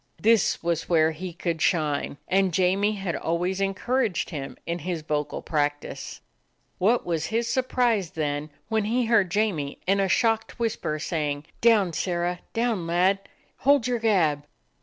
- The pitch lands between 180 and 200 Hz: Yes, medium, 185 Hz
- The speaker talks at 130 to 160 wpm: Yes, average, 150 wpm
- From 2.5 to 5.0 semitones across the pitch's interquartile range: No, wide, 5.4 semitones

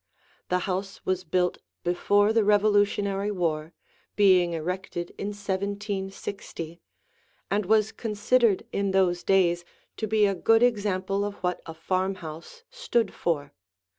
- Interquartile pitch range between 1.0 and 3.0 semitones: Yes, narrow, 2.5 semitones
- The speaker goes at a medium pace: No, slow, 125 wpm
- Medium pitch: No, high, 195 Hz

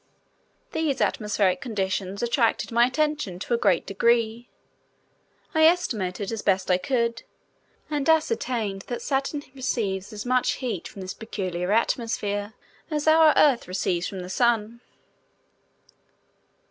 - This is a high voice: Yes, high, 230 Hz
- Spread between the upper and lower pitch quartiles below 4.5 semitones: No, wide, 5.4 semitones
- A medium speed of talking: No, slow, 125 wpm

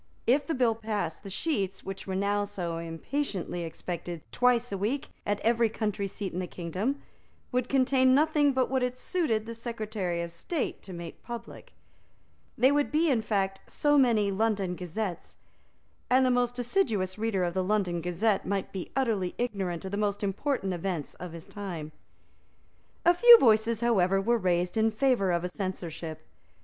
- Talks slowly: No, average, 175 wpm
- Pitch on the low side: No, high, 205 Hz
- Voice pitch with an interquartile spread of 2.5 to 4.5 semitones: No, average, 5.1 semitones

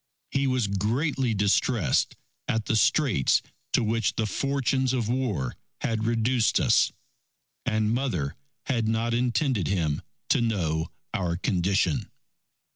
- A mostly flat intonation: No, average, 4.4 semitones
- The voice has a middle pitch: No, low, 115 Hz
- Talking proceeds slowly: Yes, slow, 120 wpm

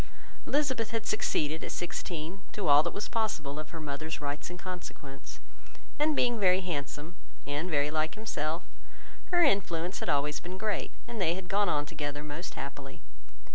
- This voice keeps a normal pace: Yes, average, 170 wpm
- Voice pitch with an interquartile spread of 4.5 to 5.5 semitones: Yes, average, 5.1 semitones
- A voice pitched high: No, medium, 165 Hz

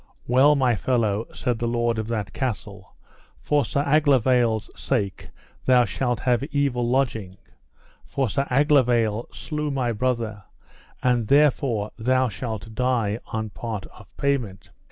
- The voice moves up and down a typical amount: Yes, average, 3.2 semitones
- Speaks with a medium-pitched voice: No, low, 120 Hz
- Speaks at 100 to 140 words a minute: Yes, slow, 135 wpm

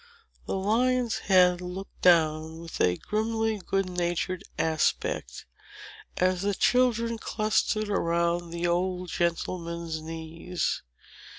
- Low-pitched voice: No, medium, 180 Hz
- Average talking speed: No, slow, 105 wpm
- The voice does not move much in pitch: No, average, 3.5 semitones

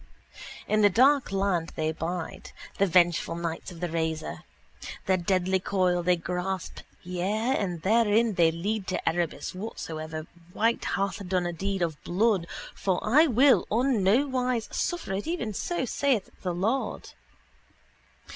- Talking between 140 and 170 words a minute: Yes, average, 145 wpm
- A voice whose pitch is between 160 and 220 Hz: Yes, high, 190 Hz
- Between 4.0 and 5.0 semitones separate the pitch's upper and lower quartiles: Yes, average, 4.4 semitones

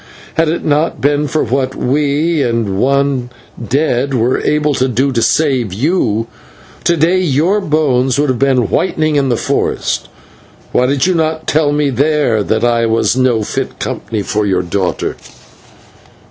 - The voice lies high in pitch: No, low, 135 Hz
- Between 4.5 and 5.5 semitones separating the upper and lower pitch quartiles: No, average, 4.1 semitones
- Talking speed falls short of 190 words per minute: Yes, average, 160 wpm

